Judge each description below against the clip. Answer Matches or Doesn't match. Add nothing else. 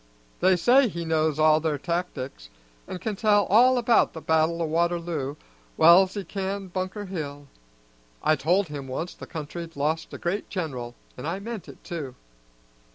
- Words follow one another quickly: Doesn't match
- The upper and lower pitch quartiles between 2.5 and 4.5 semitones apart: Matches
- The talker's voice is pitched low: Doesn't match